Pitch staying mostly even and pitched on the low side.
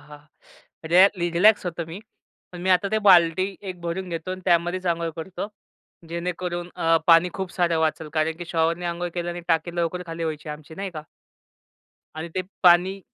No: narrow, 1.6 semitones; medium, 175 Hz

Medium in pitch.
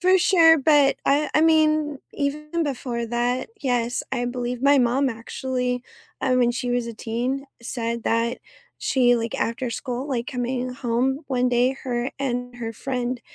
No: very high, 250 Hz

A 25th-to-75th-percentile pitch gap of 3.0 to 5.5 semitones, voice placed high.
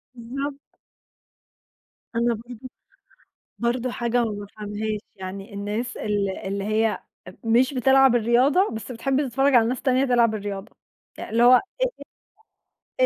Yes: average, 3.3 semitones; high, 235 Hz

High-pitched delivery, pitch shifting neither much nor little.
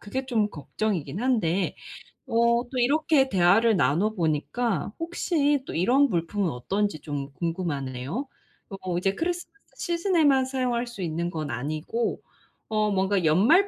No: high, 205 Hz; wide, 7.6 semitones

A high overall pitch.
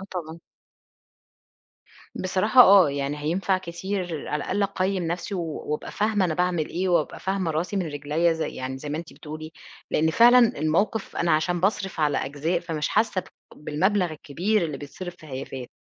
No: medium, 170 Hz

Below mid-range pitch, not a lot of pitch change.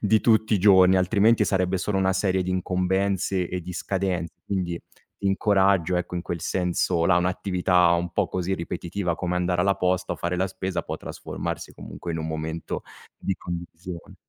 Yes: very low, 90 Hz; narrow, 1.6 semitones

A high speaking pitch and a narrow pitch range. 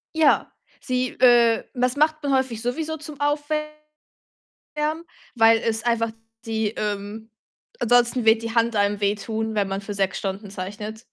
No: high, 230 Hz; average, 3.7 semitones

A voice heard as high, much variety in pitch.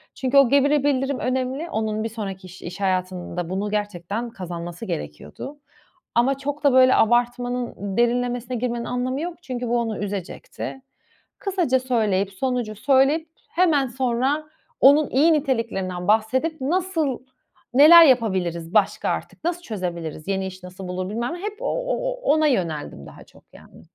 Yes: high, 245 Hz; wide, 6.2 semitones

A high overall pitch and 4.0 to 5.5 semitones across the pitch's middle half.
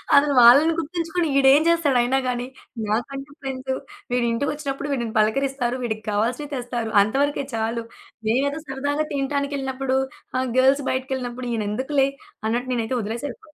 No: very high, 265 Hz; average, 2.9 semitones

